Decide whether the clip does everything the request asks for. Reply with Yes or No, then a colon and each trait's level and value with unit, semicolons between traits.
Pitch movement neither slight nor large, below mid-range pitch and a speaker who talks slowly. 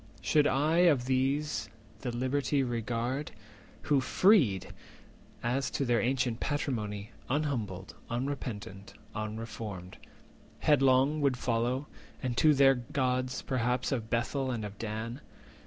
Yes: average, 3.3 semitones; low, 125 Hz; slow, 120 wpm